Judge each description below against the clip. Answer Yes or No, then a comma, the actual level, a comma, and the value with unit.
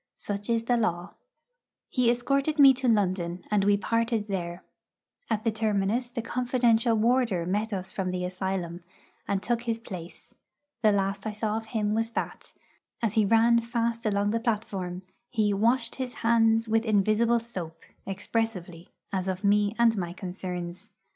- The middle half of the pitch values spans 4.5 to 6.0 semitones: No, average, 3.3 semitones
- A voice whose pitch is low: No, high, 215 Hz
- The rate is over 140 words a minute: Yes, average, 160 wpm